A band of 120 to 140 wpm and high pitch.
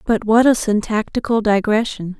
Yes: slow, 135 wpm; high, 220 Hz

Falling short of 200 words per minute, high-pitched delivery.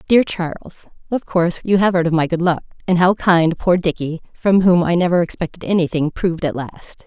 No: average, 185 wpm; medium, 175 Hz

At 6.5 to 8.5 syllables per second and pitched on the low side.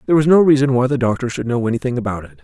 Yes: 7.9 syllables/s; low, 130 Hz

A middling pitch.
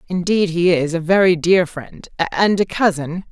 Yes: medium, 175 Hz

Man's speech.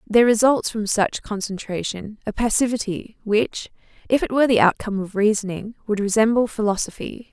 No: female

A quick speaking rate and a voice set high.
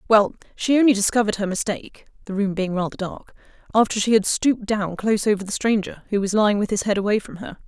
Yes: fast, 225 wpm; high, 205 Hz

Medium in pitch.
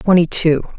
Yes: medium, 170 Hz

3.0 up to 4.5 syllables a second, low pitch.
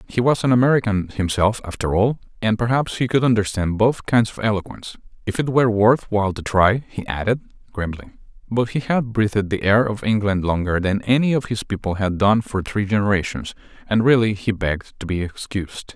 No: 5.6 syllables/s; low, 105 Hz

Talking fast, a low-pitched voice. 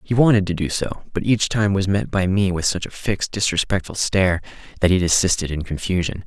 Yes: fast, 220 wpm; very low, 95 Hz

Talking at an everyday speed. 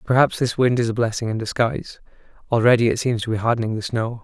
No: fast, 225 wpm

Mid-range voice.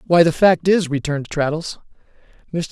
Yes: medium, 160 Hz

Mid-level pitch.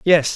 Yes: medium, 160 Hz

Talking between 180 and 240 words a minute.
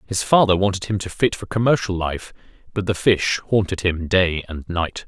Yes: average, 200 wpm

